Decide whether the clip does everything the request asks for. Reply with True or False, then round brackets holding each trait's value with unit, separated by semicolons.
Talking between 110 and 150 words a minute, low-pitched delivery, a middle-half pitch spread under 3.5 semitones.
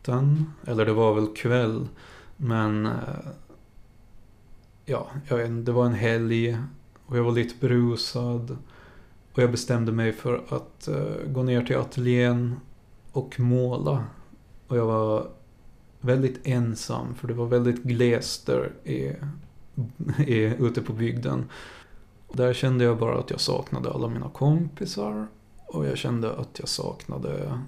True (130 wpm; 120 Hz; 2.4 semitones)